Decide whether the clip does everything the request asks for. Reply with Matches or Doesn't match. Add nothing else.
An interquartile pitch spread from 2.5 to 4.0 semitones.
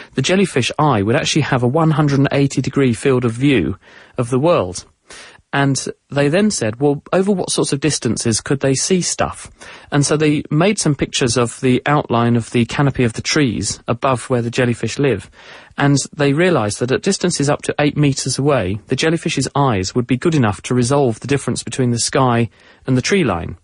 Matches